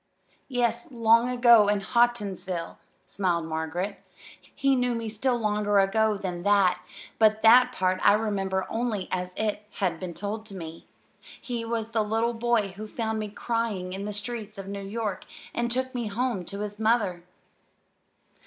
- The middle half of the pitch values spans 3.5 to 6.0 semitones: No, average, 3.1 semitones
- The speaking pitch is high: Yes, high, 210 Hz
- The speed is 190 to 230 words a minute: No, average, 165 wpm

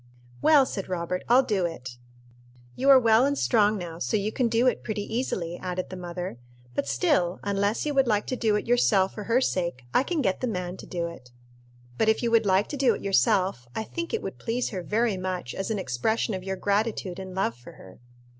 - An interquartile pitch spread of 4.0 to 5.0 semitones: Yes, average, 4.4 semitones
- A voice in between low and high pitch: No, high, 200 Hz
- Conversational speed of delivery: No, fast, 230 wpm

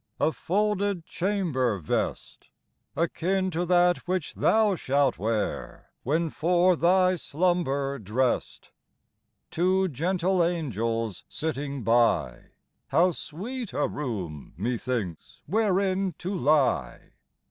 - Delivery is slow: Yes, slow, 105 wpm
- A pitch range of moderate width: No, wide, 6.5 semitones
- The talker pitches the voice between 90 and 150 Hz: No, medium, 165 Hz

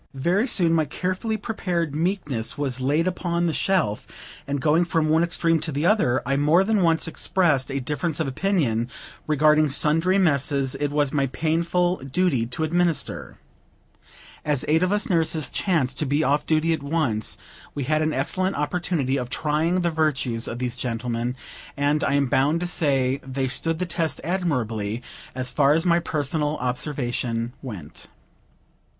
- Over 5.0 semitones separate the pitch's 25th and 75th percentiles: No, average, 4.2 semitones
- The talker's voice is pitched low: No, medium, 150 Hz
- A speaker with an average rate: Yes, average, 165 wpm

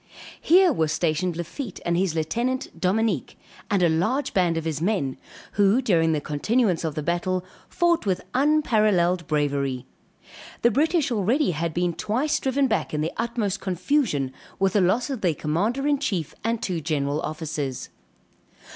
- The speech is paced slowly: No, average, 160 wpm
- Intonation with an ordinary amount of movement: No, wide, 6.8 semitones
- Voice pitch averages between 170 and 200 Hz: Yes, medium, 185 Hz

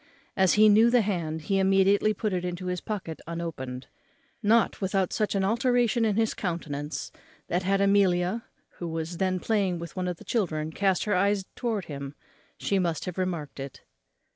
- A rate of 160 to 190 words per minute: Yes, average, 180 wpm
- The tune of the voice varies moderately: Yes, average, 3.4 semitones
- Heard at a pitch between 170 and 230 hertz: Yes, medium, 185 Hz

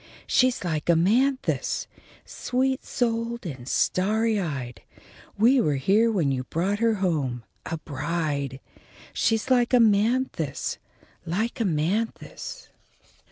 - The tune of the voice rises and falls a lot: Yes, wide, 7.0 semitones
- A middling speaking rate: No, slow, 105 wpm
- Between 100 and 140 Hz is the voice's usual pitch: No, high, 200 Hz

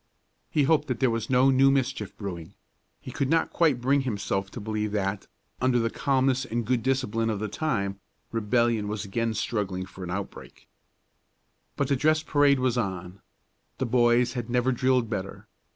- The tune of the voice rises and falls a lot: No, average, 4.2 semitones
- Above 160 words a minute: Yes, average, 175 wpm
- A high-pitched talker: No, low, 120 Hz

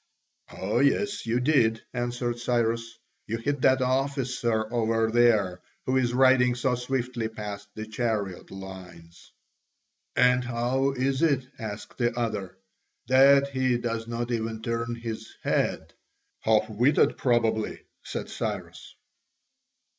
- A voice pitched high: No, low, 120 Hz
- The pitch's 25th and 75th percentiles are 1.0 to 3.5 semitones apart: Yes, narrow, 2.5 semitones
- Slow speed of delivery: Yes, slow, 125 wpm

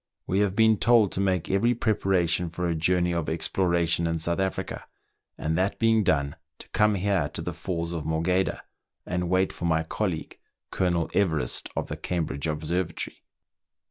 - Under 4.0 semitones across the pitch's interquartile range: Yes, average, 2.8 semitones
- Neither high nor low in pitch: No, very low, 90 Hz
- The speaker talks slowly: No, average, 175 wpm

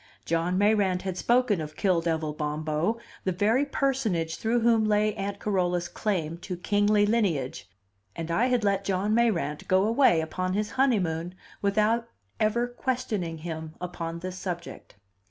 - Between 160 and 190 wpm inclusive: No, average, 150 wpm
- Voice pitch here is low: No, high, 190 Hz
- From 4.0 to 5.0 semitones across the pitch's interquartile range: Yes, average, 4.5 semitones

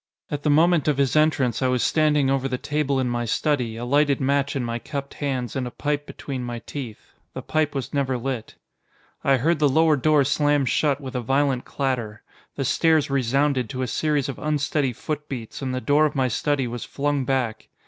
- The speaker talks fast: Yes, fast, 210 wpm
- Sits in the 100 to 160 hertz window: Yes, low, 135 Hz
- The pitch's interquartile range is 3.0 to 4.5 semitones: No, narrow, 2.6 semitones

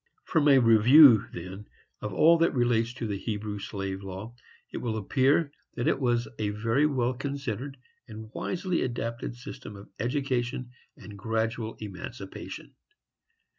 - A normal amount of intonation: Yes, average, 4.0 semitones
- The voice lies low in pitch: Yes, low, 115 Hz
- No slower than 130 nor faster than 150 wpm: Yes, average, 140 wpm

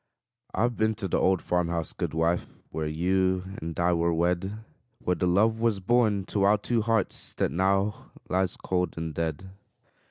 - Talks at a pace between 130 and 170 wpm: No, average, 180 wpm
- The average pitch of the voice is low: Yes, very low, 95 Hz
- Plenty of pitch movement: No, average, 3.5 semitones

